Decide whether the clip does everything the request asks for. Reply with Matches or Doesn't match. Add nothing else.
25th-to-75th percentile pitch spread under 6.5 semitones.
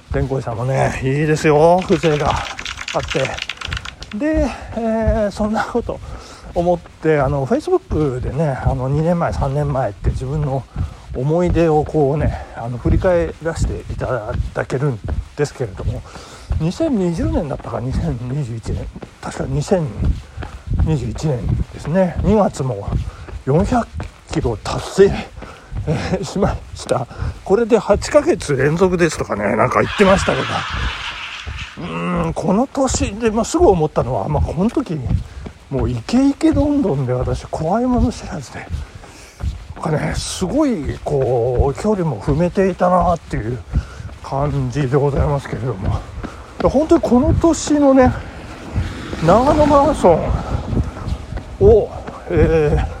Doesn't match